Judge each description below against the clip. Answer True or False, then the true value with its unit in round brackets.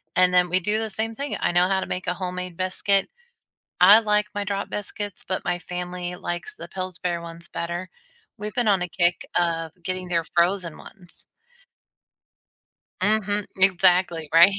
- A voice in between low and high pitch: True (180 Hz)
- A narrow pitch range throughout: True (2.3 semitones)